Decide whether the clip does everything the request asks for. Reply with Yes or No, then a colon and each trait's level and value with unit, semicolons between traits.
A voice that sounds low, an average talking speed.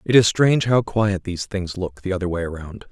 No: low, 100 Hz; fast, 245 wpm